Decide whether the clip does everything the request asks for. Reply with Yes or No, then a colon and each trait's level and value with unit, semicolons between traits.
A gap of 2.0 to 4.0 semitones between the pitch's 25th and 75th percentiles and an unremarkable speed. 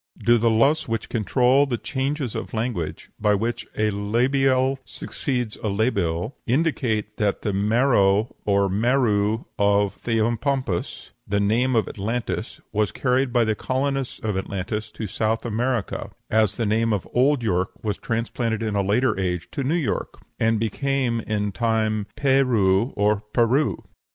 Yes: average, 3.6 semitones; average, 150 wpm